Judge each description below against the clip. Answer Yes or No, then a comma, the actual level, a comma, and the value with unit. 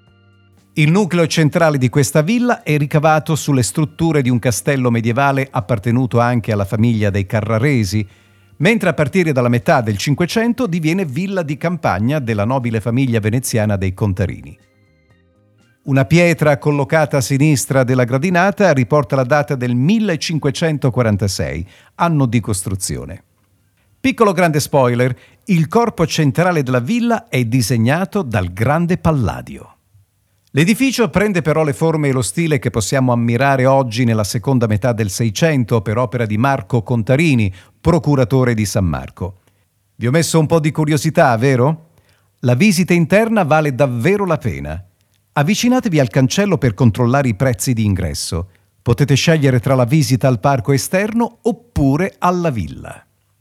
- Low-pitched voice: Yes, low, 130 Hz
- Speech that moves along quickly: No, average, 140 wpm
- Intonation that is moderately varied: No, wide, 6.0 semitones